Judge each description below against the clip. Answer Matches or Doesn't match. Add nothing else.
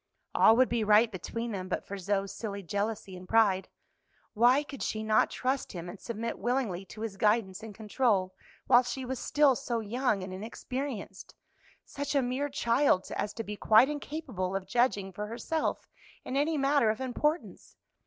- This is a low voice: Doesn't match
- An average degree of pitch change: Matches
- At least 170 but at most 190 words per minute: Matches